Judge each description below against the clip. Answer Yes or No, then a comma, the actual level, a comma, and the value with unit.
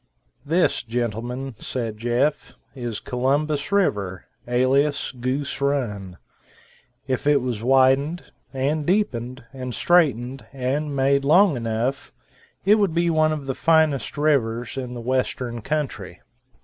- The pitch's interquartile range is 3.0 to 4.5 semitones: Yes, average, 3.6 semitones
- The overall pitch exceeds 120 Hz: Yes, low, 135 Hz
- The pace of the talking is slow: Yes, slow, 125 wpm